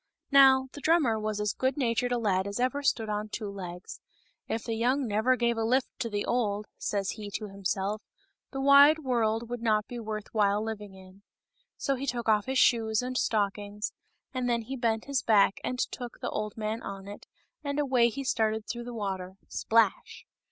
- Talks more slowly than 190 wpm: No, fast, 205 wpm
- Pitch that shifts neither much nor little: Yes, average, 3.3 semitones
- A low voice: No, high, 225 Hz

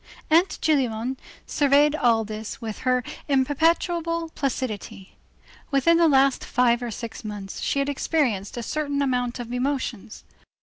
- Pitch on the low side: No, very high, 260 Hz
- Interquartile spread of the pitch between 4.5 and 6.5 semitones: No, average, 3.9 semitones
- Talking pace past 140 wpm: No, slow, 135 wpm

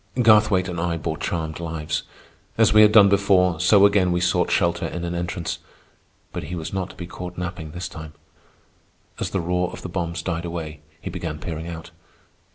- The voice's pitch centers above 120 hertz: No, very low, 85 Hz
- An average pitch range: No, narrow, 1.9 semitones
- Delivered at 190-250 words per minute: Yes, average, 195 wpm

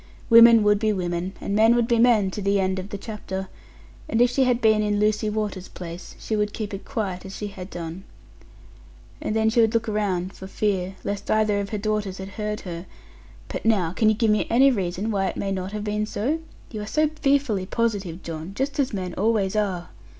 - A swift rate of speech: Yes, fast, 225 wpm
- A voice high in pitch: Yes, high, 210 Hz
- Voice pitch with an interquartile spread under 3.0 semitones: Yes, narrow, 2.6 semitones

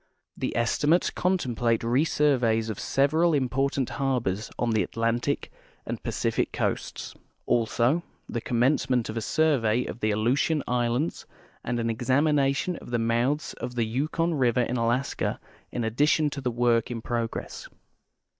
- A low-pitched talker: Yes, low, 125 Hz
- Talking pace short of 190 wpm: Yes, average, 140 wpm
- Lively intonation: No, average, 3.5 semitones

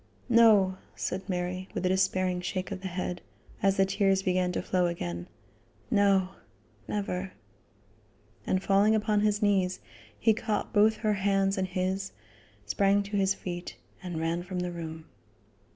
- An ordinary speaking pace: Yes, average, 150 wpm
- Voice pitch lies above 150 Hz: Yes, high, 190 Hz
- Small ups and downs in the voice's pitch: Yes, narrow, 1.8 semitones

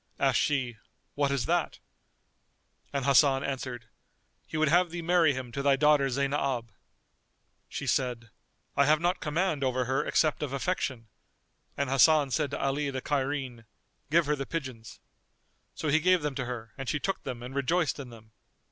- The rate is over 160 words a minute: Yes, average, 175 wpm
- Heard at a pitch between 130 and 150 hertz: Yes, medium, 140 Hz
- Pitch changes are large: No, average, 2.7 semitones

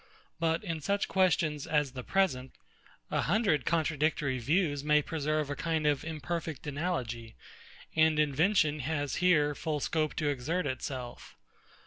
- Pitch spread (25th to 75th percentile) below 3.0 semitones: Yes, narrow, 2.4 semitones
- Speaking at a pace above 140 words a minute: No, slow, 135 wpm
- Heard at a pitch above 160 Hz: No, medium, 155 Hz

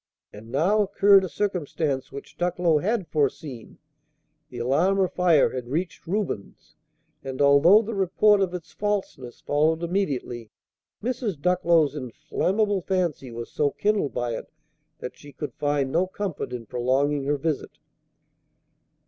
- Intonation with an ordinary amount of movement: No, wide, 5.8 semitones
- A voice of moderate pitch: Yes, medium, 160 Hz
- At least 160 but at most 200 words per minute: No, average, 140 wpm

